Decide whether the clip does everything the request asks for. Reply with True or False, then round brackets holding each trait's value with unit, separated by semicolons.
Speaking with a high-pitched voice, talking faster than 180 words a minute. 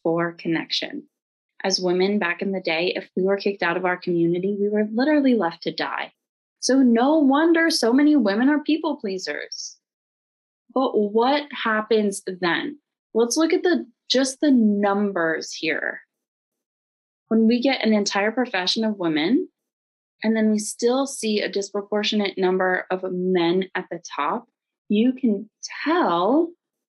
False (215 Hz; 150 wpm)